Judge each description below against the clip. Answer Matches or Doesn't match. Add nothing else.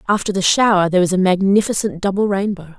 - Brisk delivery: Doesn't match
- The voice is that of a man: Doesn't match